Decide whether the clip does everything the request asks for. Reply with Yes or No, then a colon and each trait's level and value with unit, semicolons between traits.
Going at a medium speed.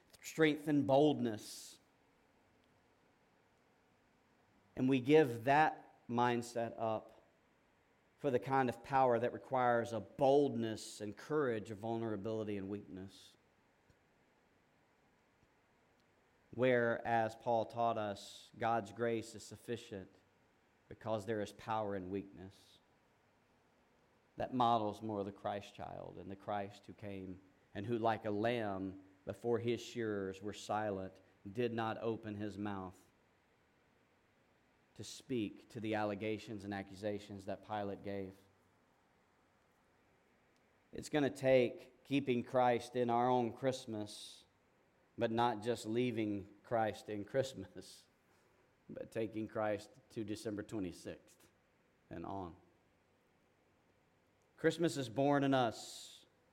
No: slow, 110 wpm